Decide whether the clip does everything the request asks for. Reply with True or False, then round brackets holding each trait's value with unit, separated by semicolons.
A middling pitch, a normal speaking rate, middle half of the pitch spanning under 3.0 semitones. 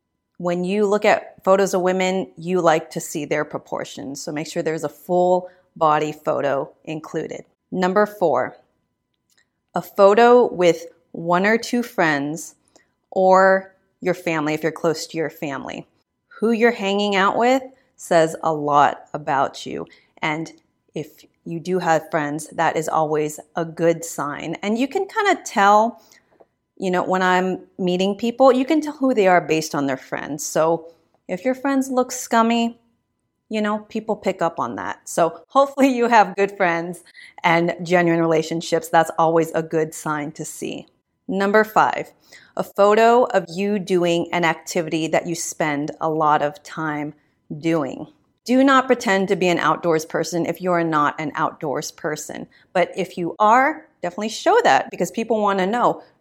False (180 Hz; 165 wpm; 4.5 semitones)